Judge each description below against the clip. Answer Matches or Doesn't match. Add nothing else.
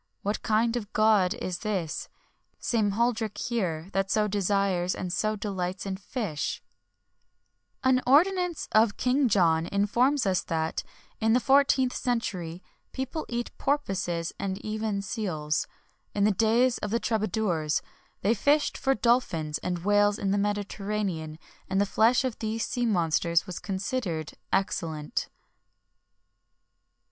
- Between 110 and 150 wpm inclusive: Matches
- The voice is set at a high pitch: Matches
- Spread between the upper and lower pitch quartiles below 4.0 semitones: Doesn't match